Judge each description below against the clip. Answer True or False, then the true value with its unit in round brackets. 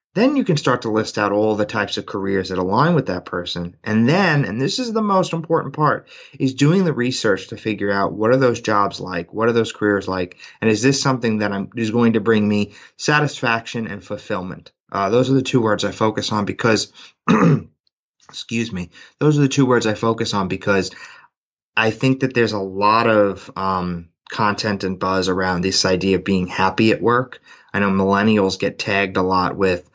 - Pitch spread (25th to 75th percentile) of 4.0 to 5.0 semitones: True (4.3 semitones)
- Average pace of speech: False (210 wpm)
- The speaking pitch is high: False (105 Hz)